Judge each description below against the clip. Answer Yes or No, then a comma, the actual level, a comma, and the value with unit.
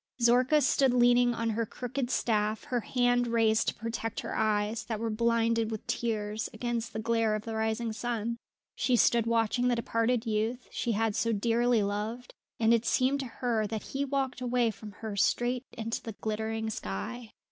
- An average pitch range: No, narrow, 1.8 semitones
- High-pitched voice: Yes, high, 230 Hz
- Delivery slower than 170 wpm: No, average, 180 wpm